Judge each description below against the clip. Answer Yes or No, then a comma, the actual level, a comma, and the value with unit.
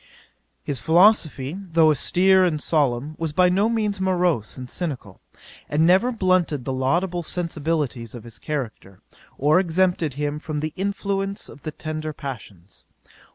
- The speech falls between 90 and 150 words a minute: Yes, average, 145 wpm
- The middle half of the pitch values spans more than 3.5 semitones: Yes, average, 4.9 semitones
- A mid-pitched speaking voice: Yes, medium, 155 Hz